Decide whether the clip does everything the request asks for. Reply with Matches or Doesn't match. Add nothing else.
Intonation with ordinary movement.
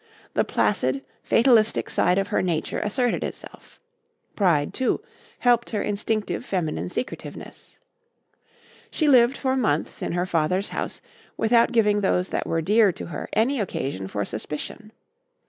Doesn't match